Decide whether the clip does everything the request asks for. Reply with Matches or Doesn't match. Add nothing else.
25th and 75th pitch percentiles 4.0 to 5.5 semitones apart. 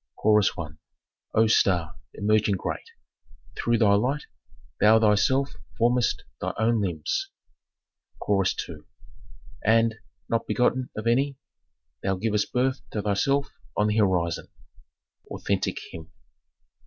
Doesn't match